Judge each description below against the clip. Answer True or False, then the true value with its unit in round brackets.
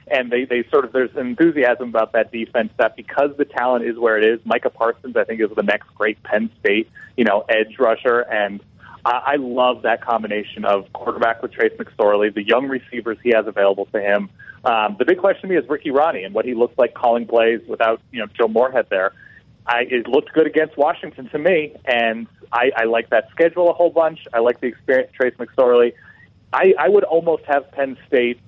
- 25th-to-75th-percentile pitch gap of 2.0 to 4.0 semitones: False (4.4 semitones)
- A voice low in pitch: True (120 Hz)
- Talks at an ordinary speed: False (215 wpm)